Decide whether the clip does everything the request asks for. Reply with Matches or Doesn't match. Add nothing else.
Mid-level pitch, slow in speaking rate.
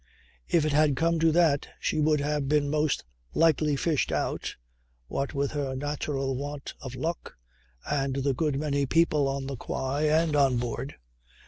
Doesn't match